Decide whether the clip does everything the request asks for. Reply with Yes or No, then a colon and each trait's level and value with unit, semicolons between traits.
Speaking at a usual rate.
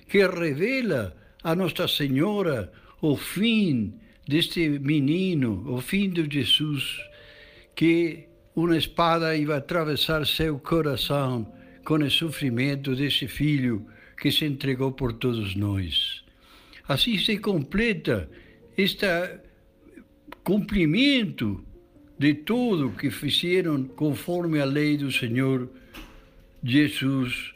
No: slow, 100 wpm